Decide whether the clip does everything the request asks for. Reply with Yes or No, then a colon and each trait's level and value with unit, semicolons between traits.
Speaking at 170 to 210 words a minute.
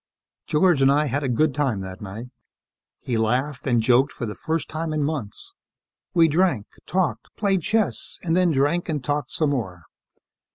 Yes: average, 175 wpm